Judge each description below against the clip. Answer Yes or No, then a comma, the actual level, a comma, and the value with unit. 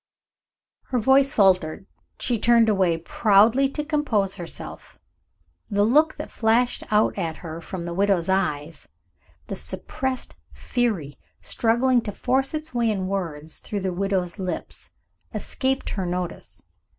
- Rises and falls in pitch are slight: No, average, 5.3 semitones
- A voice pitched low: No, high, 205 Hz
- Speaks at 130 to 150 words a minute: Yes, slow, 135 wpm